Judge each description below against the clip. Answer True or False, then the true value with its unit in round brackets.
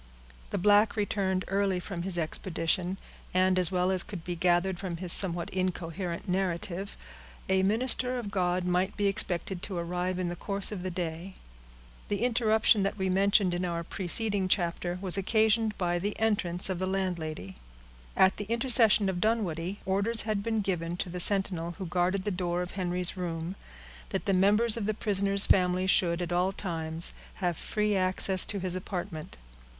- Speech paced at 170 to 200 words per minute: True (175 wpm)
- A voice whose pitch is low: False (185 Hz)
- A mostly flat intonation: True (2.3 semitones)